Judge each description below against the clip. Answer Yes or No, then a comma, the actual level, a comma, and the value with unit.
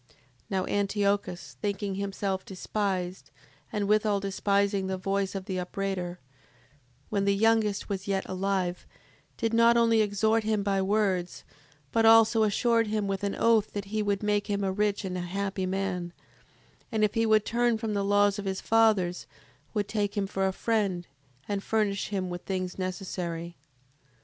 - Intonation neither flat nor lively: No, narrow, 1.9 semitones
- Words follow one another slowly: No, average, 170 wpm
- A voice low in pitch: No, high, 200 Hz